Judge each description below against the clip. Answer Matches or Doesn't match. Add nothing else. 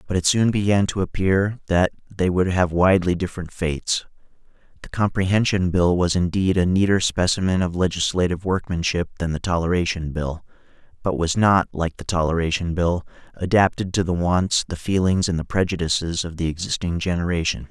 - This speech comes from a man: Matches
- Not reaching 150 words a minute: Doesn't match